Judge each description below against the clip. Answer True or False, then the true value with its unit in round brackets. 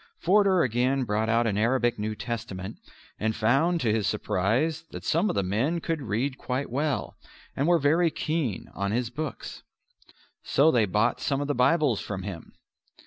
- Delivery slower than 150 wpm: False (175 wpm)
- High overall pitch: False (125 Hz)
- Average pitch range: False (5.9 semitones)